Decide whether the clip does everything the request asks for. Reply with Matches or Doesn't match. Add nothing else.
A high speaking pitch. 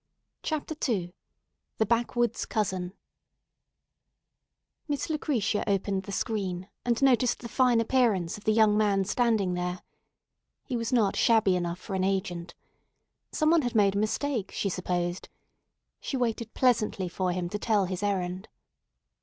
Matches